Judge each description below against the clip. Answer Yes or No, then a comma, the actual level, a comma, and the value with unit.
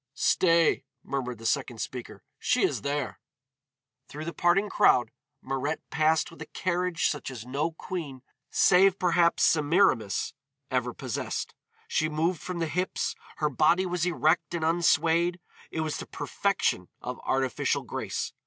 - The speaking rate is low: No, average, 145 wpm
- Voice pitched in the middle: Yes, medium, 160 Hz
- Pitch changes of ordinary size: Yes, average, 4.1 semitones